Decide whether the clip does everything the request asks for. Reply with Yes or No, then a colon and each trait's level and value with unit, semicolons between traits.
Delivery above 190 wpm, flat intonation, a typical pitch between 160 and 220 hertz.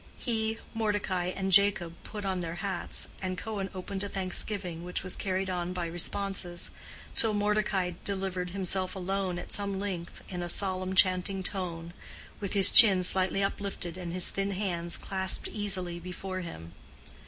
No: average, 155 wpm; narrow, 1.8 semitones; high, 190 Hz